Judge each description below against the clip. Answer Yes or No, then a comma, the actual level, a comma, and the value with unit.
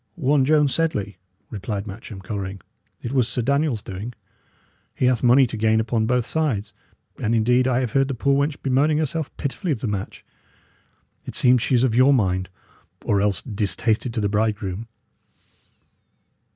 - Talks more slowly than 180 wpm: Yes, average, 165 wpm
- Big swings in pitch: No, average, 4.5 semitones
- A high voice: No, low, 120 Hz